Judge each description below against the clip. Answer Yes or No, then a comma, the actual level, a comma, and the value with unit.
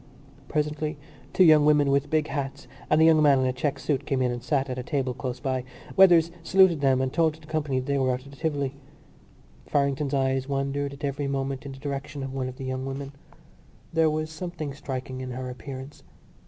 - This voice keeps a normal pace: No, fast, 220 wpm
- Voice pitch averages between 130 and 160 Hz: Yes, medium, 140 Hz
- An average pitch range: No, narrow, 2.3 semitones